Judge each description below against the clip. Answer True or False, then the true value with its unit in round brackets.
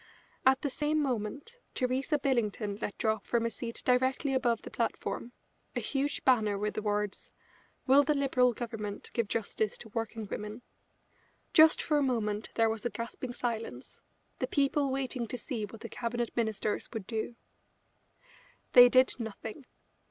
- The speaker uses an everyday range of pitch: True (3.3 semitones)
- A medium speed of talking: True (160 wpm)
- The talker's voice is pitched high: True (235 Hz)